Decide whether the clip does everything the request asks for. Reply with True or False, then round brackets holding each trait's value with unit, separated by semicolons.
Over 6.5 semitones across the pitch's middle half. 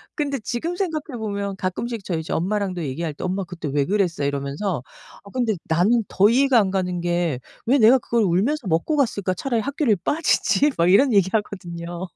False (5.6 semitones)